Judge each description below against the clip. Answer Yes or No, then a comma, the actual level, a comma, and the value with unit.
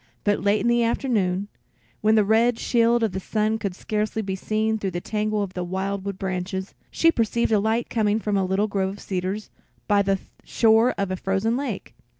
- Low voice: No, high, 210 Hz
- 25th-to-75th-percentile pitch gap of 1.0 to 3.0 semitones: Yes, narrow, 2.4 semitones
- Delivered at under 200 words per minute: No, fast, 205 wpm